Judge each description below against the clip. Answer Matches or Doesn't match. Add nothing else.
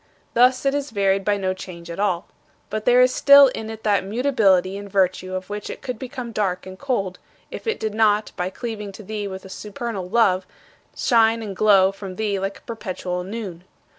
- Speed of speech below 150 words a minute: Doesn't match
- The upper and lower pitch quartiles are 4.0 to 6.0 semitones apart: Doesn't match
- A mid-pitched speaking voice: Doesn't match